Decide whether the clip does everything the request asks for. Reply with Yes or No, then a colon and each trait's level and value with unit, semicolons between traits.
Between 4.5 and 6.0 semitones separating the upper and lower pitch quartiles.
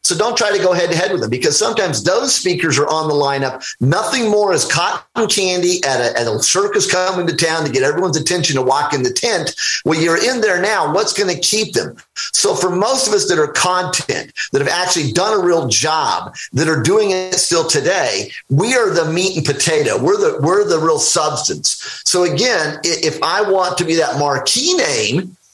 Yes: average, 5.3 semitones